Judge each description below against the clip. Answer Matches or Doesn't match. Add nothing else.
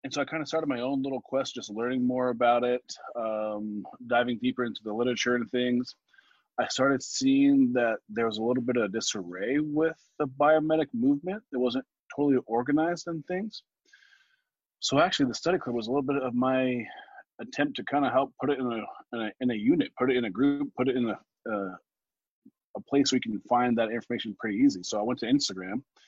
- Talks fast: Matches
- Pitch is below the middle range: Matches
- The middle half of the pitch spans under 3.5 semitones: Doesn't match